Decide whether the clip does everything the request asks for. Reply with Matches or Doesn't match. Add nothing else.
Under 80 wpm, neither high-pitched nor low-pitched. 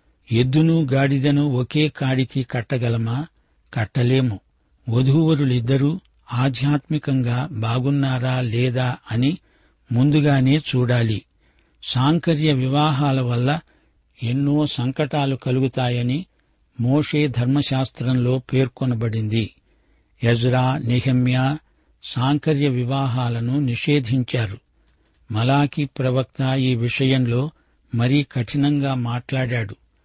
Doesn't match